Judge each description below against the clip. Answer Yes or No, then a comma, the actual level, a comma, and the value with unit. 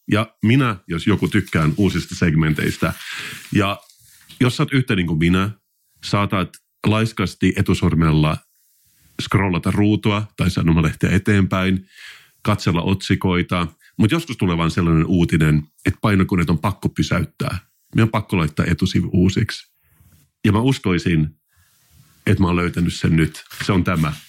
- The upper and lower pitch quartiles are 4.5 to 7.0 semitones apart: No, average, 3.7 semitones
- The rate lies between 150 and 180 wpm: No, average, 135 wpm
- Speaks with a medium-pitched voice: No, very low, 95 Hz